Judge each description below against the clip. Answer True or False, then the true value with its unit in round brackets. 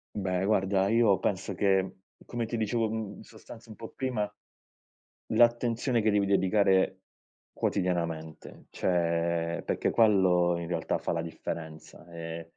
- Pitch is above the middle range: False (95 Hz)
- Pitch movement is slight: False (4.3 semitones)